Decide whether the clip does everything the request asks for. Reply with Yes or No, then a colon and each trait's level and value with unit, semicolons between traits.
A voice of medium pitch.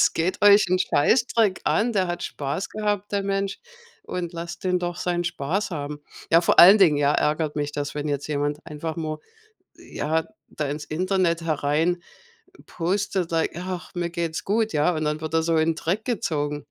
Yes: medium, 170 Hz